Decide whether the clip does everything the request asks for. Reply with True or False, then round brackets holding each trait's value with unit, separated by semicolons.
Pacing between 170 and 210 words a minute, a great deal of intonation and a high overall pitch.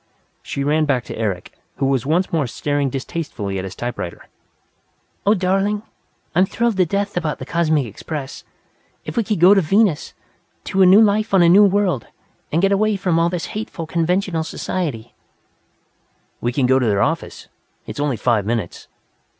False (180 wpm; 6.6 semitones; 165 Hz)